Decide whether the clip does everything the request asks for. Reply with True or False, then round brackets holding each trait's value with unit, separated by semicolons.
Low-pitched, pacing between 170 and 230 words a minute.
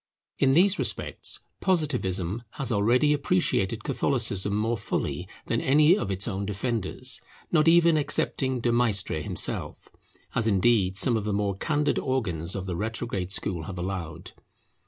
False (110 Hz; 145 wpm)